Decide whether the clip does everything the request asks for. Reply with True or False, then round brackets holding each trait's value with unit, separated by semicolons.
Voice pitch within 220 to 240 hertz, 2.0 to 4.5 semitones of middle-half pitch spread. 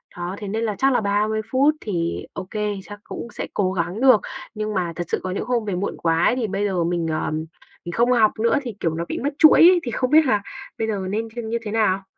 False (210 Hz; 4.0 semitones)